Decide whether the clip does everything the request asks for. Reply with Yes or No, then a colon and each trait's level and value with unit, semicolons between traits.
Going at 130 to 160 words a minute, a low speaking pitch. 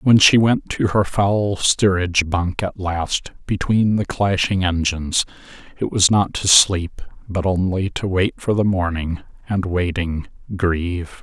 Yes: average, 155 wpm; very low, 95 Hz